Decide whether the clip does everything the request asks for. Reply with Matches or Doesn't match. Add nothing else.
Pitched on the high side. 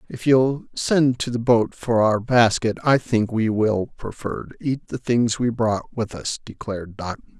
Doesn't match